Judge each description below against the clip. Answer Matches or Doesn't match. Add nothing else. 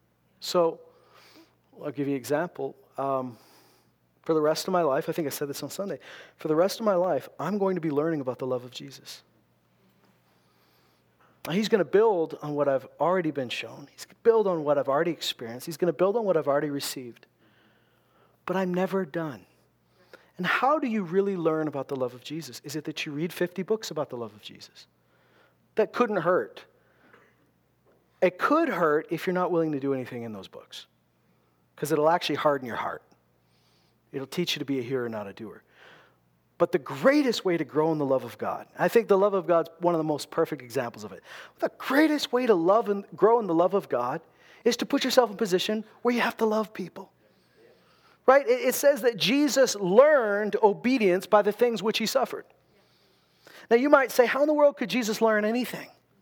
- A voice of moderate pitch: Matches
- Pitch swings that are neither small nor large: Doesn't match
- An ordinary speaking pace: Doesn't match